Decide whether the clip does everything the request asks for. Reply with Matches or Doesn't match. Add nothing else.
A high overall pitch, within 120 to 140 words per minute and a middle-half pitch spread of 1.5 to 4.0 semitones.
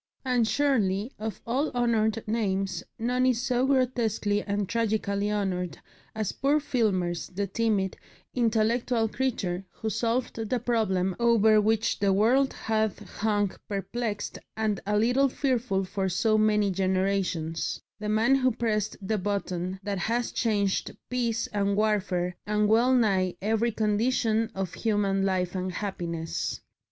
Matches